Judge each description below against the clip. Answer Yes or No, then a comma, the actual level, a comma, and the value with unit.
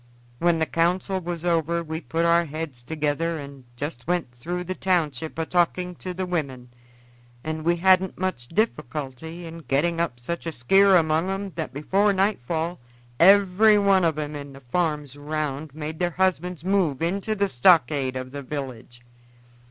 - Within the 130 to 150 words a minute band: No, average, 165 wpm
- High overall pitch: No, medium, 165 Hz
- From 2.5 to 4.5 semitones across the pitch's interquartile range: Yes, average, 3.8 semitones